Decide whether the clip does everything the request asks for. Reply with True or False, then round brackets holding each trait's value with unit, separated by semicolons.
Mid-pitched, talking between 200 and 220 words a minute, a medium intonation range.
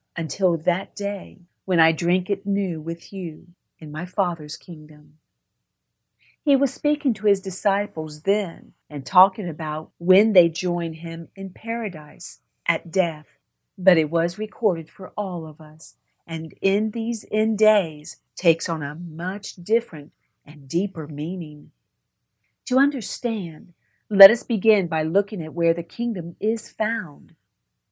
False (180 Hz; 140 wpm; 4.0 semitones)